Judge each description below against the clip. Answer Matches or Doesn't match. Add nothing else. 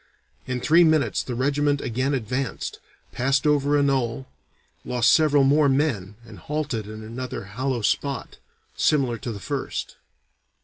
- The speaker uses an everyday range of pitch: Matches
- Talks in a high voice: Doesn't match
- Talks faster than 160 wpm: Doesn't match